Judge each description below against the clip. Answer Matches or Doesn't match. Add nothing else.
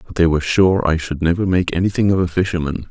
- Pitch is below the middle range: Matches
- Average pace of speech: Doesn't match